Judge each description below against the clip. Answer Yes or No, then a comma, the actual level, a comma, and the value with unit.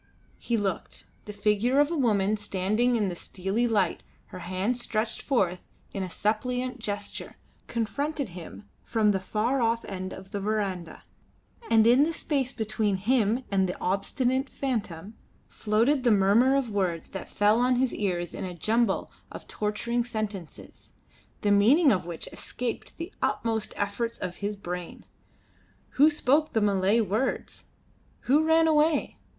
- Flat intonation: No, average, 4.2 semitones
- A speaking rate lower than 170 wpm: Yes, average, 155 wpm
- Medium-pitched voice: No, high, 215 Hz